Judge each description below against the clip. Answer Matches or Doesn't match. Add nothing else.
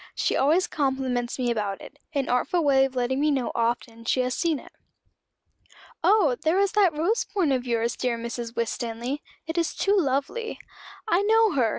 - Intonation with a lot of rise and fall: Matches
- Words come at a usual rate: Matches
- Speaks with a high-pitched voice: Matches